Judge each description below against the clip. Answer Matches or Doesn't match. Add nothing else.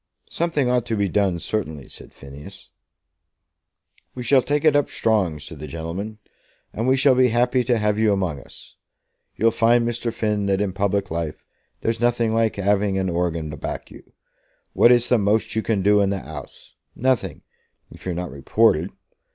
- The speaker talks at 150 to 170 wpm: Doesn't match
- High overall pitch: Doesn't match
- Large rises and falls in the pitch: Doesn't match